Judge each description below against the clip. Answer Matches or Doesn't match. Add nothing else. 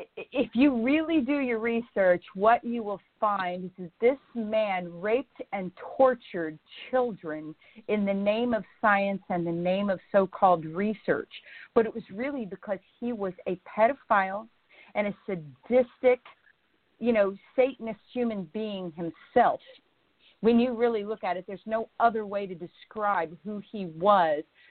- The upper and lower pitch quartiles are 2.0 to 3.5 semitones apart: Doesn't match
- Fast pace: Doesn't match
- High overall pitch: Matches